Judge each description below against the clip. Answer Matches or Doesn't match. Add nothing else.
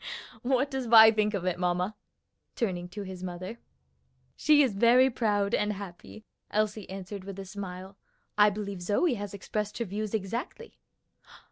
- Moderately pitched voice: Doesn't match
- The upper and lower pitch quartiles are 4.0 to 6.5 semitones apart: Doesn't match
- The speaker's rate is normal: Matches